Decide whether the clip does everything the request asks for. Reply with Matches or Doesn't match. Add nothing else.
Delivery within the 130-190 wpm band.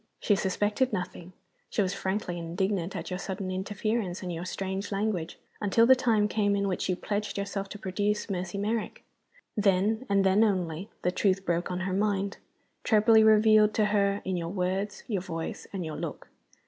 Matches